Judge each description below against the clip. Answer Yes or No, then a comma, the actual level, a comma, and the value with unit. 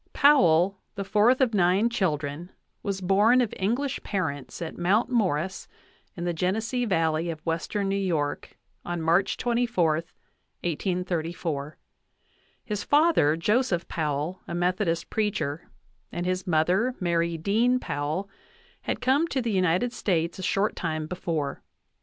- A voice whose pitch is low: No, medium, 180 Hz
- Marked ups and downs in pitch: No, average, 4.5 semitones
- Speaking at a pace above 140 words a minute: No, slow, 135 wpm